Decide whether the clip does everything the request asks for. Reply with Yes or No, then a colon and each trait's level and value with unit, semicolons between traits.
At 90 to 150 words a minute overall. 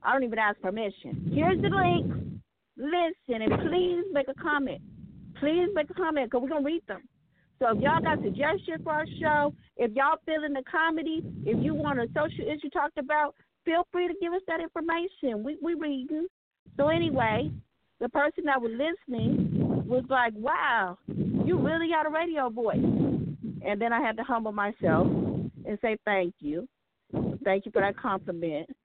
No: average, 185 wpm